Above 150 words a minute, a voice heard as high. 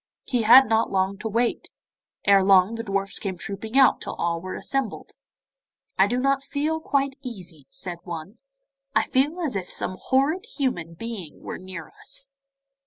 Yes: average, 165 wpm; high, 220 Hz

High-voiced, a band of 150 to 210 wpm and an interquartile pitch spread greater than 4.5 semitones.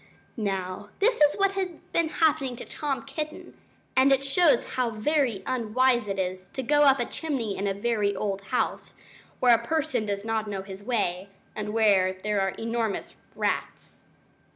Yes: high, 230 Hz; average, 175 wpm; wide, 5.4 semitones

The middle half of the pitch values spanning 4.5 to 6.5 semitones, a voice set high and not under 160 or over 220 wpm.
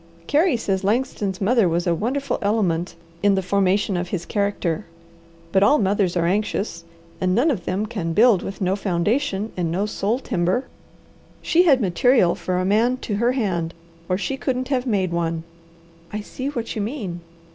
Yes: average, 4.8 semitones; high, 200 Hz; average, 180 wpm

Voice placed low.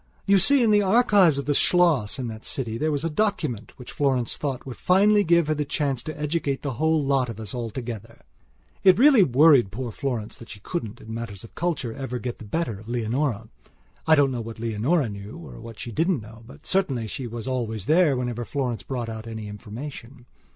Yes: low, 130 Hz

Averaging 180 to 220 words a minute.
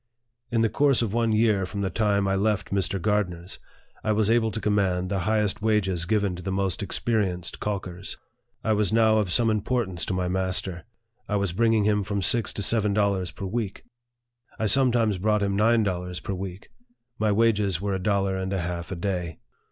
Yes: average, 200 wpm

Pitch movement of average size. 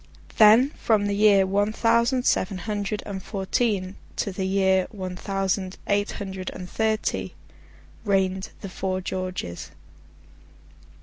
No: narrow, 2.0 semitones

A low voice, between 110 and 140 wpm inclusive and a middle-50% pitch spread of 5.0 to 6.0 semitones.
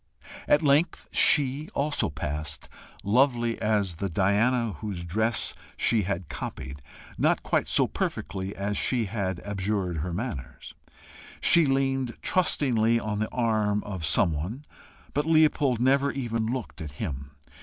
Yes: low, 110 Hz; slow, 135 wpm; wide, 5.5 semitones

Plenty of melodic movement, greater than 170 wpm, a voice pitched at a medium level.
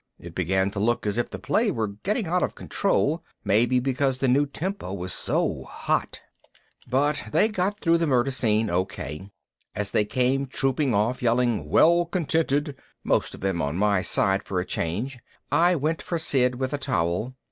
No: wide, 6.6 semitones; average, 180 wpm; low, 125 Hz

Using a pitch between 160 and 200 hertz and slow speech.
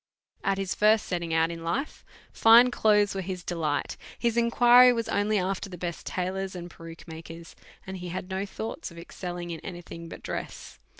No: medium, 185 Hz; average, 190 wpm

